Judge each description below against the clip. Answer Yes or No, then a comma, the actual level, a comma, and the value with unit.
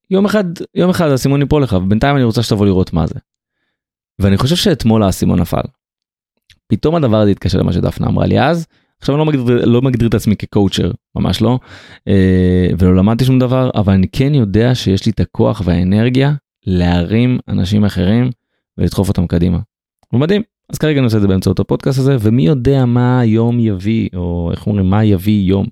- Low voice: Yes, low, 110 Hz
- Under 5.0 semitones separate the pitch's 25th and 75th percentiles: No, average, 5.3 semitones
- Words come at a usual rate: No, fast, 185 wpm